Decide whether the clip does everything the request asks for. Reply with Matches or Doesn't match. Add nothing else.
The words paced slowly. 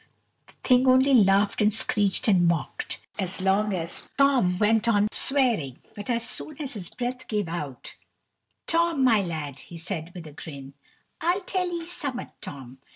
Doesn't match